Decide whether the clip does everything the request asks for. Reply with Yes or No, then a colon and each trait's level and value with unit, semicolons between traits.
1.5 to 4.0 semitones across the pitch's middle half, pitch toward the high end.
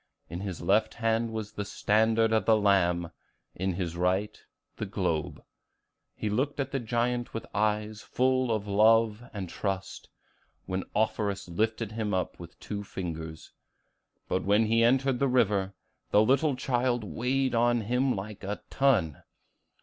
No: average, 3.5 semitones; low, 110 Hz